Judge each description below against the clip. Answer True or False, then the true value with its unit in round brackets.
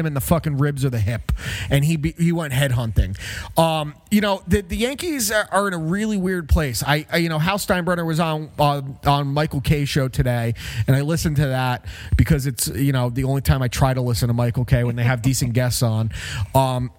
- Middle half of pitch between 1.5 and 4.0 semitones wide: False (4.7 semitones)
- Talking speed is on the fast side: True (240 wpm)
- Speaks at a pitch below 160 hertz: True (140 Hz)